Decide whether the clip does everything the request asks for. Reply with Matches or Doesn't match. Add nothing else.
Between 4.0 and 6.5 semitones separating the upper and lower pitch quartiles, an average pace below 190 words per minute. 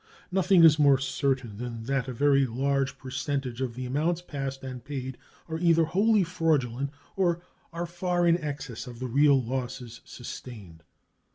Matches